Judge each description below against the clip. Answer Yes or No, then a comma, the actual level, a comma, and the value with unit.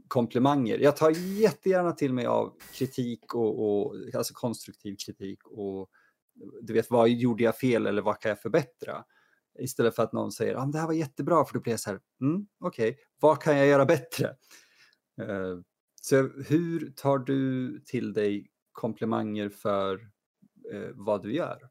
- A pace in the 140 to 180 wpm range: Yes, average, 175 wpm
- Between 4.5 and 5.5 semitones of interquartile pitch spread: Yes, average, 5.1 semitones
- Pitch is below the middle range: Yes, low, 120 Hz